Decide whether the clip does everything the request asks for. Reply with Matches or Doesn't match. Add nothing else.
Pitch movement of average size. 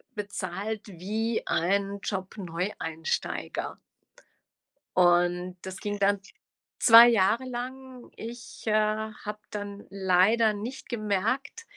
Matches